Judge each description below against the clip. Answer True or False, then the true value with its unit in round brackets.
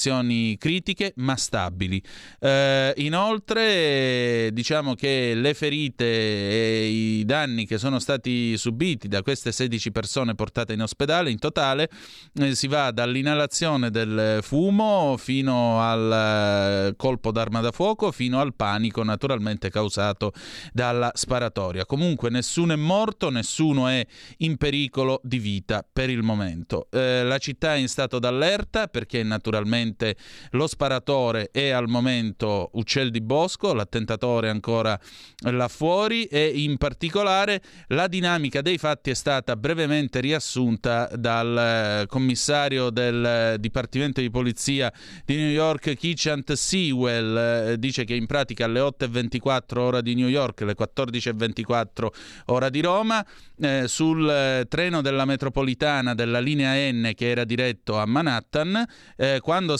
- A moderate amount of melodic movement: True (4.1 semitones)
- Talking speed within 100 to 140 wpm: True (130 wpm)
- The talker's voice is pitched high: False (125 Hz)